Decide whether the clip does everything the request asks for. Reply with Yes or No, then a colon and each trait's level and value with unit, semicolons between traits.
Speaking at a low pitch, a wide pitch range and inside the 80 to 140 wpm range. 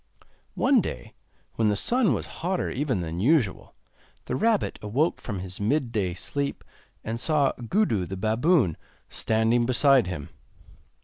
Yes: low, 115 Hz; wide, 6.7 semitones; slow, 135 wpm